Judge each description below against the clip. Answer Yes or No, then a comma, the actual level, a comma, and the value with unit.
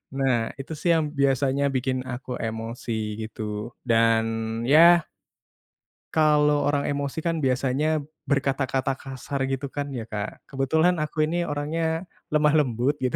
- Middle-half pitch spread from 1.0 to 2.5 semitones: No, average, 3.3 semitones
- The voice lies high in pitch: No, medium, 140 Hz